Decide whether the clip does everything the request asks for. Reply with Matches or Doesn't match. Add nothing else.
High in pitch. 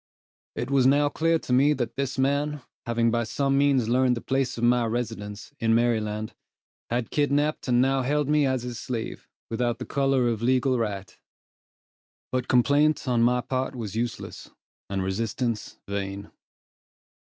Doesn't match